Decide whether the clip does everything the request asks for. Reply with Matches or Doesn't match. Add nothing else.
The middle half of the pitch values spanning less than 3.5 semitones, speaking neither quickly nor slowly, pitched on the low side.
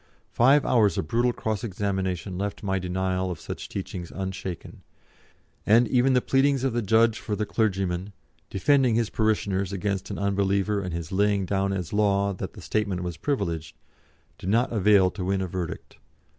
Matches